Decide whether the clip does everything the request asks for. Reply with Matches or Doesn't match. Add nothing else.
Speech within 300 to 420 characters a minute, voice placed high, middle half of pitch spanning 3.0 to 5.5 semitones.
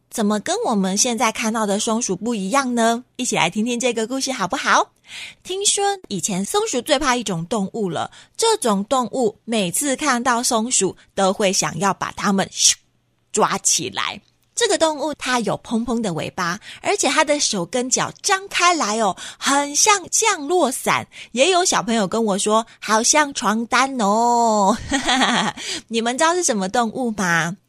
Doesn't match